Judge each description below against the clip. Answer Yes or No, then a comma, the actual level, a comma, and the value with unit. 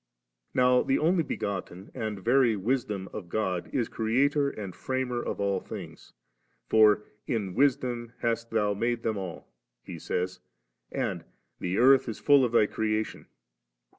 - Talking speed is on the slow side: No, average, 155 wpm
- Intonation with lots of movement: No, average, 3.8 semitones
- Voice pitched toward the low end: Yes, low, 115 Hz